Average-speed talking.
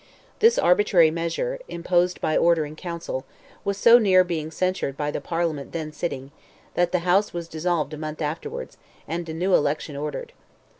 Yes: average, 160 wpm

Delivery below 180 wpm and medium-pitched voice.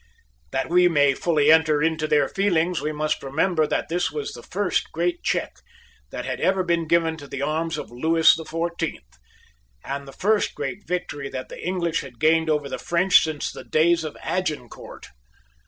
No: average, 185 wpm; medium, 160 Hz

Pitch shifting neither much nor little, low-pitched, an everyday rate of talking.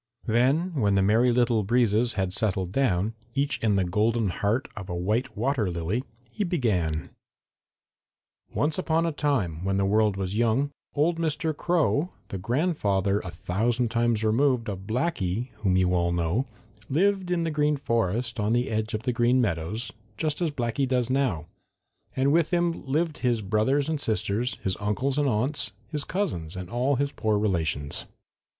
No: wide, 6.2 semitones; low, 115 Hz; average, 170 wpm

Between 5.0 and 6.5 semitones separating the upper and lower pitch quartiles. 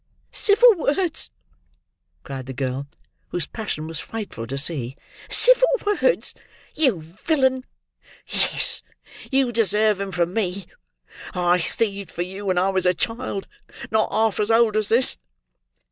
Yes: wide, 5.4 semitones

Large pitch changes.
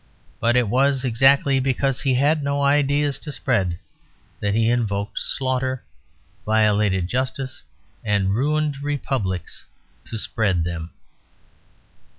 No: average, 5.0 semitones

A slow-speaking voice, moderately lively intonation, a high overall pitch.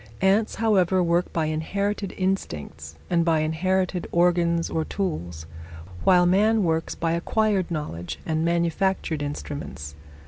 No: slow, 125 wpm; average, 3.4 semitones; medium, 170 Hz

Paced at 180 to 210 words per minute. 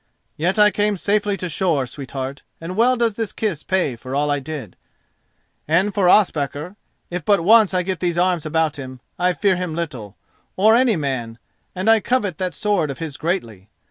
Yes: average, 195 wpm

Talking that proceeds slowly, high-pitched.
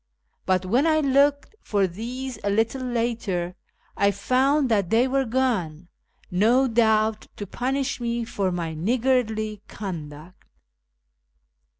Yes: slow, 120 wpm; high, 225 Hz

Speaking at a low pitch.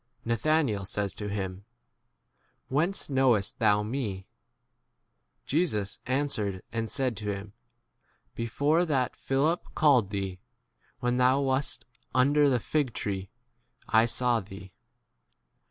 Yes: low, 120 Hz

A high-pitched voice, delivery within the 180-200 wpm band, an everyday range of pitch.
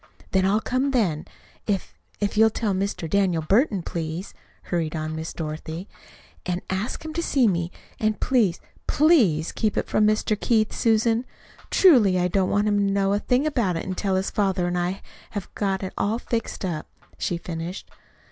Yes: high, 195 Hz; average, 185 wpm; average, 3.8 semitones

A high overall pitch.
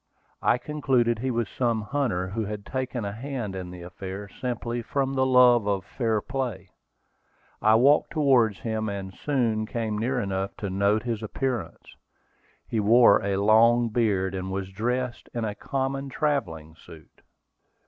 No: low, 115 Hz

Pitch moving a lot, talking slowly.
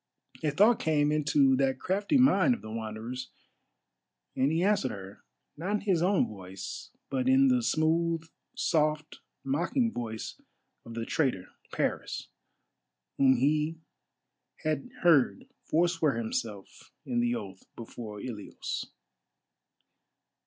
Yes: wide, 5.9 semitones; slow, 120 wpm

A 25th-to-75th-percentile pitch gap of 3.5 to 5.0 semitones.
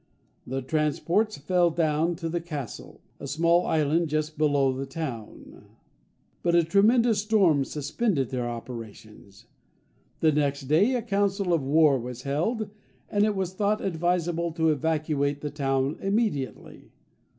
Yes: average, 4.6 semitones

